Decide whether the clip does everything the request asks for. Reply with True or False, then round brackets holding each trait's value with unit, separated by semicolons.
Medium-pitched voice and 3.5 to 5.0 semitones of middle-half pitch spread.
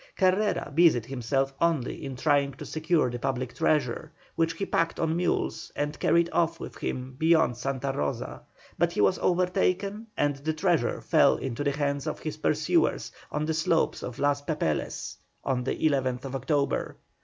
True (145 Hz; 3.9 semitones)